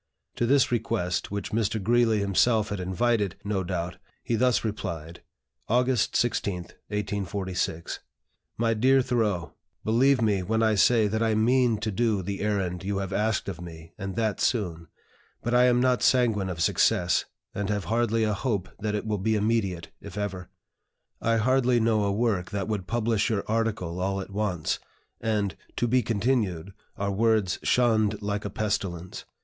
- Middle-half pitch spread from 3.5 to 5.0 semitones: No, average, 2.9 semitones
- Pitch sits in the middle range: No, low, 105 Hz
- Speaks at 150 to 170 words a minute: Yes, average, 165 wpm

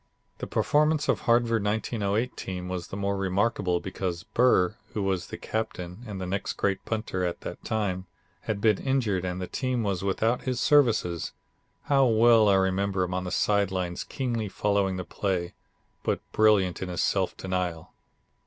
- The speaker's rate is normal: Yes, average, 170 wpm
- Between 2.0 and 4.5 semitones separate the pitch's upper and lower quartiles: Yes, average, 3.4 semitones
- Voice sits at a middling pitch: No, low, 100 Hz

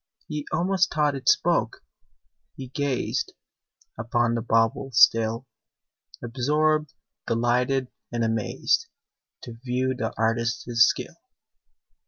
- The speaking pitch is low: Yes, low, 125 Hz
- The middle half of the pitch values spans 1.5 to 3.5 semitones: Yes, average, 3.2 semitones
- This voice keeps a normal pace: No, slow, 100 wpm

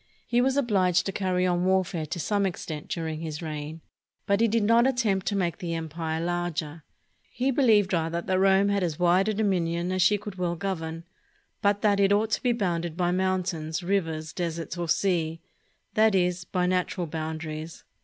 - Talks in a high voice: No, medium, 180 Hz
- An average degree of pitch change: Yes, average, 3.3 semitones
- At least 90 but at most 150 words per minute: No, average, 185 wpm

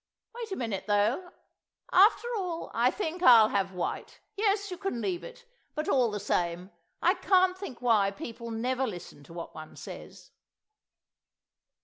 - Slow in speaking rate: No, average, 155 wpm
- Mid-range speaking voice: No, very high, 250 Hz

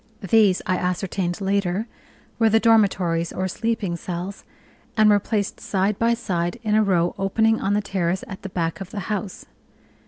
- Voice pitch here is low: No, high, 195 Hz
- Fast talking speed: No, average, 175 wpm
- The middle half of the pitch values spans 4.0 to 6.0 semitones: No, average, 3.0 semitones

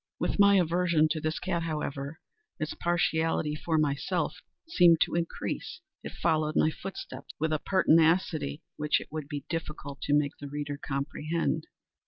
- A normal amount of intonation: No, narrow, 2.3 semitones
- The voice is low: No, medium, 155 Hz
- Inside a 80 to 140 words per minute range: No, average, 155 wpm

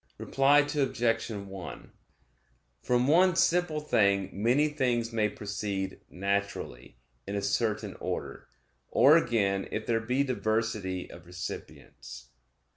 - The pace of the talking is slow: Yes, slow, 115 wpm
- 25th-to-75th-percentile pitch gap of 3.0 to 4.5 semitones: No, average, 5.1 semitones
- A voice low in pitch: Yes, low, 110 Hz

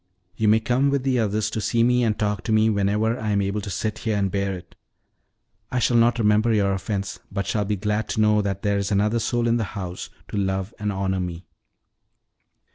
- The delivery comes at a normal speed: No, fast, 225 wpm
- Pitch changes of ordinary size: No, narrow, 2.2 semitones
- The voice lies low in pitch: Yes, low, 105 Hz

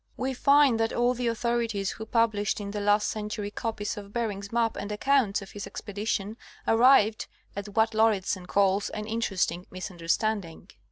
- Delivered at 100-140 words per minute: No, average, 165 wpm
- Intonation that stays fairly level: Yes, narrow, 2.3 semitones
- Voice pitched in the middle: No, high, 210 Hz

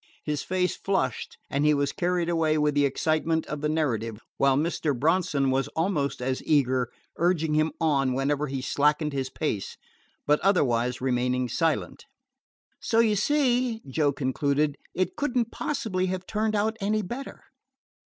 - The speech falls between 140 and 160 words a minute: Yes, average, 155 wpm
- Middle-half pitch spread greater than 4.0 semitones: Yes, average, 5.2 semitones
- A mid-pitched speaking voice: Yes, medium, 150 Hz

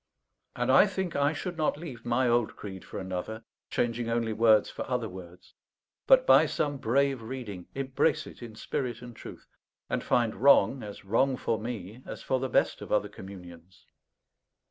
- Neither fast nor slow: Yes, average, 175 wpm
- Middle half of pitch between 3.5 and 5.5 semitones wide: Yes, average, 4.1 semitones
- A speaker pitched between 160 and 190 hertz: No, low, 120 Hz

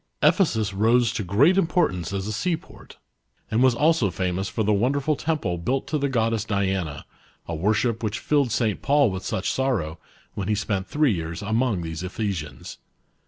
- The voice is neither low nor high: No, low, 110 Hz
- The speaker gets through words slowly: No, average, 170 wpm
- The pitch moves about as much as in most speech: No, wide, 5.8 semitones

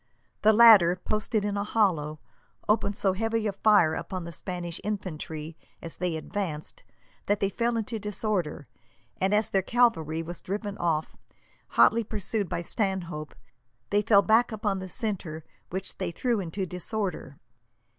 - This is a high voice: Yes, high, 195 Hz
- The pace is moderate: Yes, average, 150 wpm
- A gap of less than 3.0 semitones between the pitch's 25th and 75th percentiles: No, average, 3.8 semitones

